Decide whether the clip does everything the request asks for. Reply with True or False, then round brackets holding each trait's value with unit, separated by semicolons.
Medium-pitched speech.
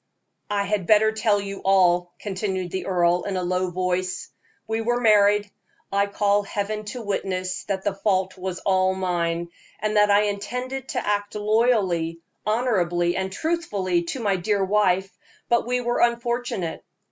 False (200 Hz)